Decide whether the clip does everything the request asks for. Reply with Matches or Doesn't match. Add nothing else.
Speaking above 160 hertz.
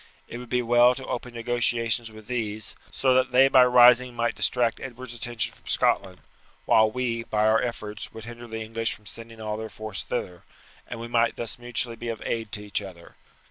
Doesn't match